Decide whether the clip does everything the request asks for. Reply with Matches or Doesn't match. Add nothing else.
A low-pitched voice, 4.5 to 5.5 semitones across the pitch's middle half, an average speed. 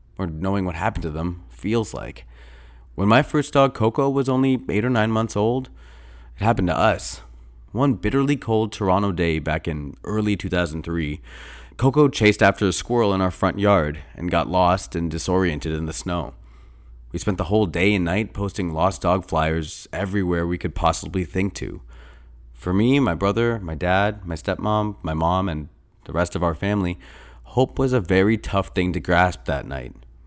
Matches